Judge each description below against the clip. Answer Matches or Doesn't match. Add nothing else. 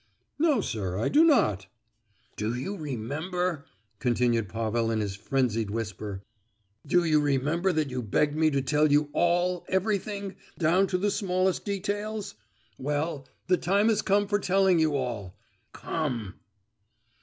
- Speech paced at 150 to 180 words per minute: Doesn't match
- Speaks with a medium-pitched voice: Matches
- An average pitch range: Doesn't match